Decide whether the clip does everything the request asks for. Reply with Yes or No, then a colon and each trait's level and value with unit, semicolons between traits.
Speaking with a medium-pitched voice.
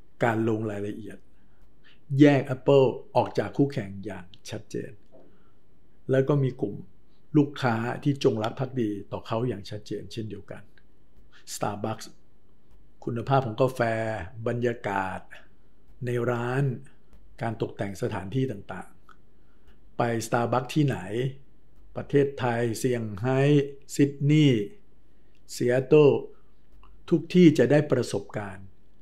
No: low, 120 Hz